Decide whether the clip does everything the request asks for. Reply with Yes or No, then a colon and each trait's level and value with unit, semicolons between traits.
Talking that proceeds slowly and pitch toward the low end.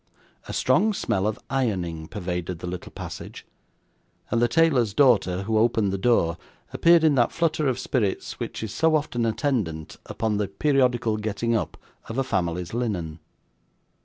No: average, 160 wpm; low, 110 Hz